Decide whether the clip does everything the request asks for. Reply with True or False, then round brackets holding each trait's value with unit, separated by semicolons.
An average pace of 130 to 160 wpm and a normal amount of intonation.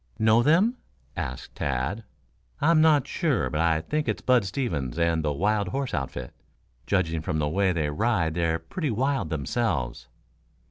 False (155 wpm; 8.5 semitones)